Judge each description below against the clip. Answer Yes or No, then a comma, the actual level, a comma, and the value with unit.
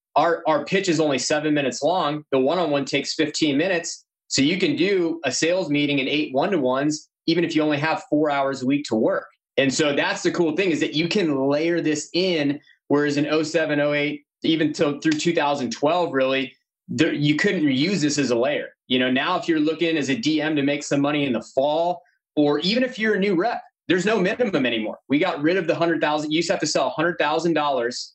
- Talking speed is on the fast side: Yes, fast, 230 wpm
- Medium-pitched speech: Yes, medium, 155 Hz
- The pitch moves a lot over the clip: No, average, 2.8 semitones